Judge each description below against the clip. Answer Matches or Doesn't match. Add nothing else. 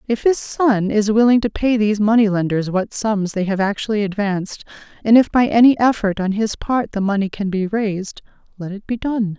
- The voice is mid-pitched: Doesn't match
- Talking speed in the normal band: Doesn't match